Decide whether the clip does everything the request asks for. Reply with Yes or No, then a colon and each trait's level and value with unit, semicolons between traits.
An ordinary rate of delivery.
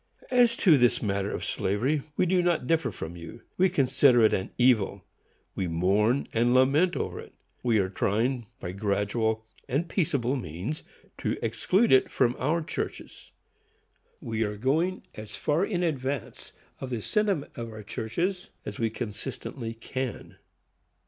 Yes: average, 155 wpm